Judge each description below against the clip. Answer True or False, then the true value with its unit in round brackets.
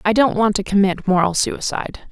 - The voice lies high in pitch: True (205 Hz)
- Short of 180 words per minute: False (200 wpm)